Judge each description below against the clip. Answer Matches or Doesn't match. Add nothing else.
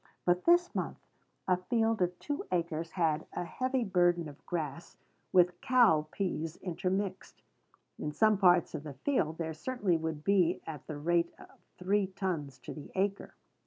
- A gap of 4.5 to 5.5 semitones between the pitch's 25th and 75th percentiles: Doesn't match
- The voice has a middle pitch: Matches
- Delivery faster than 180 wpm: Doesn't match